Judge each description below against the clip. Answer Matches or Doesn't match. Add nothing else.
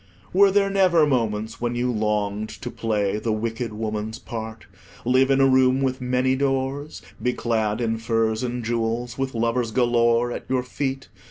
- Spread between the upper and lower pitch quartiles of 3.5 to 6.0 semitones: Doesn't match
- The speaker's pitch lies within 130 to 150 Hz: Doesn't match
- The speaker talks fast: Doesn't match